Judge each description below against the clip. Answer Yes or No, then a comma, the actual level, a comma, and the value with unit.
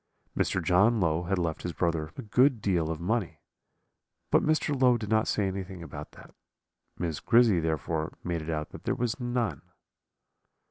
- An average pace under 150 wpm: No, average, 175 wpm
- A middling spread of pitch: No, wide, 6.0 semitones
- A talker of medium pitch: No, very low, 95 Hz